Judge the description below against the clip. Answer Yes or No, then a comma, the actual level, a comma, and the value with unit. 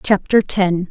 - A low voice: No, high, 190 Hz